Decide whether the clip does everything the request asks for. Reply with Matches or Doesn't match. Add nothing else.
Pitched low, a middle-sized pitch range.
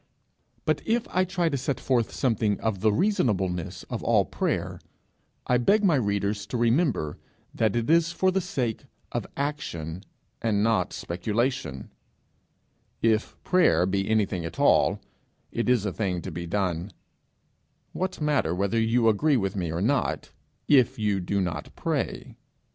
Doesn't match